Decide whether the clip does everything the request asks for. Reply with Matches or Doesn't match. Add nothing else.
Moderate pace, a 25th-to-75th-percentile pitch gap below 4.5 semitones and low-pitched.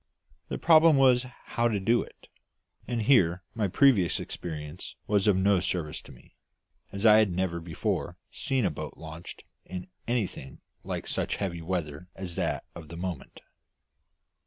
Doesn't match